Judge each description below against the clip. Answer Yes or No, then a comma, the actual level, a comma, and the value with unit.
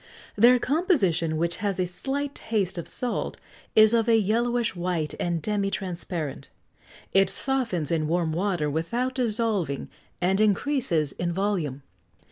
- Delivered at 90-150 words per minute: Yes, slow, 135 wpm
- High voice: Yes, high, 195 Hz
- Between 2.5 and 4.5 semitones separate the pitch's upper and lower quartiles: No, wide, 5.4 semitones